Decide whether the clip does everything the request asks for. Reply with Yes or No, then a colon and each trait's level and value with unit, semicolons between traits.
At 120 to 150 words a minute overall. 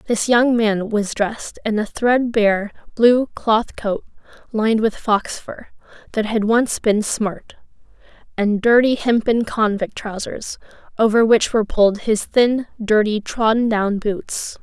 Yes: average, 145 wpm